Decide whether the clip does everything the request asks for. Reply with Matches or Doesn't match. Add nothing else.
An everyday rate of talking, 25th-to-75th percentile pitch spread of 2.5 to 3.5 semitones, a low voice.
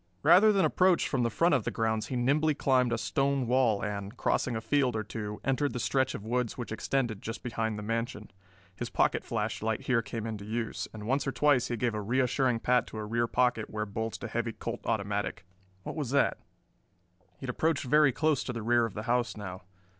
Doesn't match